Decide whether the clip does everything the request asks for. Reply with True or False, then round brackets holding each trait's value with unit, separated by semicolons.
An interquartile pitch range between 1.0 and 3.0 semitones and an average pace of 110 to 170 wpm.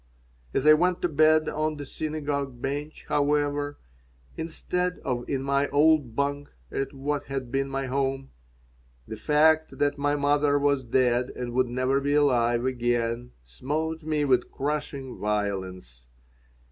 True (2.7 semitones; 145 wpm)